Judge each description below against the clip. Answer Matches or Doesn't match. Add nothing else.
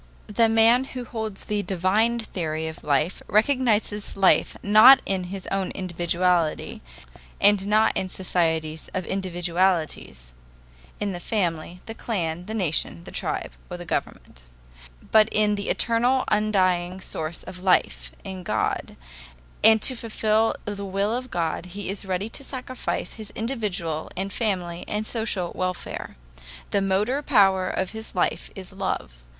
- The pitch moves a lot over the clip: Doesn't match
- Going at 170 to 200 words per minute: Doesn't match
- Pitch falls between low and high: Doesn't match